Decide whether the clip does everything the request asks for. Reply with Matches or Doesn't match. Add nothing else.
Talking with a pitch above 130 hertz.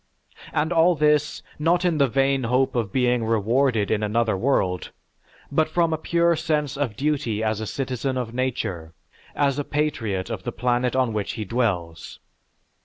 Doesn't match